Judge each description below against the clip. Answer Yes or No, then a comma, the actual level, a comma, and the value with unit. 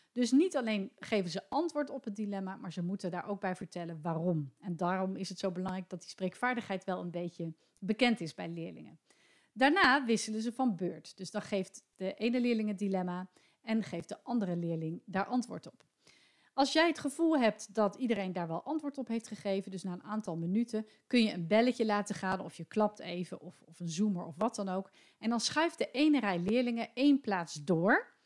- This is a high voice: Yes, high, 205 Hz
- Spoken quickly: Yes, fast, 210 wpm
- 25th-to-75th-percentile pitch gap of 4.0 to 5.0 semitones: Yes, average, 4.7 semitones